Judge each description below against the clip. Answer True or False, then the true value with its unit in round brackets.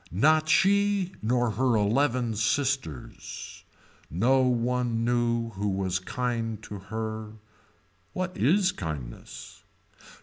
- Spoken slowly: True (100 wpm)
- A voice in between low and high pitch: False (120 Hz)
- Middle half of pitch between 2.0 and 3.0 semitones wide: False (4.1 semitones)